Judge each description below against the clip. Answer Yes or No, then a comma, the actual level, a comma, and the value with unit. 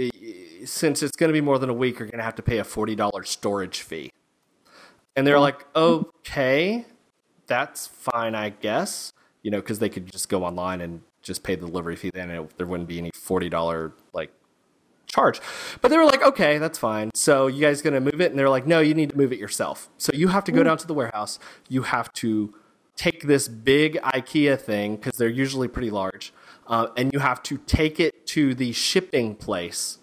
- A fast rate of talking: Yes, fast, 220 wpm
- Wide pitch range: Yes, wide, 6.2 semitones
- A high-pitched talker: No, low, 130 Hz